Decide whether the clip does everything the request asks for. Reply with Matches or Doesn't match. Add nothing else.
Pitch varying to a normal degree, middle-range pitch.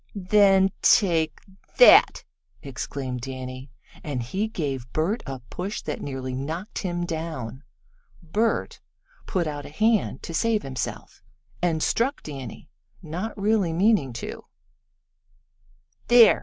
Doesn't match